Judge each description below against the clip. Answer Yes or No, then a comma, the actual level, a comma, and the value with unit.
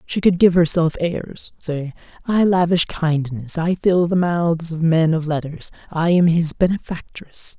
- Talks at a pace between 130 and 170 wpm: Yes, average, 165 wpm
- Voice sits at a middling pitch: Yes, medium, 165 Hz